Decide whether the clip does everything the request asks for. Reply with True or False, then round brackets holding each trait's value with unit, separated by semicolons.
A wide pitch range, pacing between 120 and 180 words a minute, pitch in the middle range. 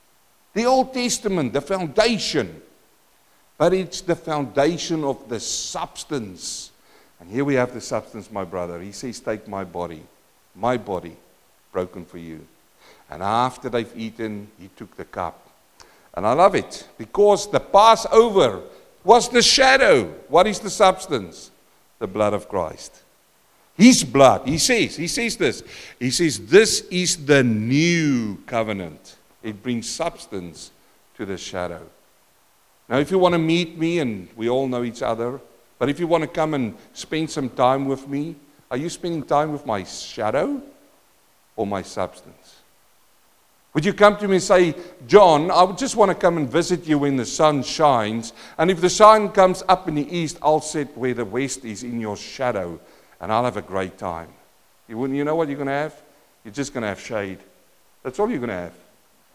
True (7.8 semitones; 175 wpm; 145 Hz)